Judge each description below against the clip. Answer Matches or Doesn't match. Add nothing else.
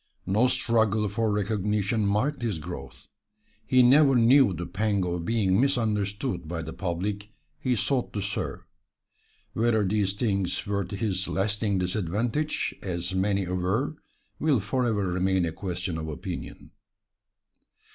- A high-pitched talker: Doesn't match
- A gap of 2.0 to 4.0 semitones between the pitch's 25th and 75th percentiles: Matches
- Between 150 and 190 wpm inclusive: Doesn't match